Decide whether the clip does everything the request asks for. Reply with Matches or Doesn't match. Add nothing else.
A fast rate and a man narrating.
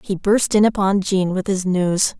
Doesn't match